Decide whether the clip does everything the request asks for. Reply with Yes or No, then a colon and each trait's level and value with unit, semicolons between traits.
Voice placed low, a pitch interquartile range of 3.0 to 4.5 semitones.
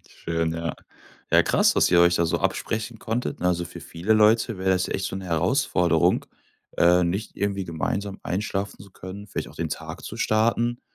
Yes: very low, 95 Hz; average, 3.6 semitones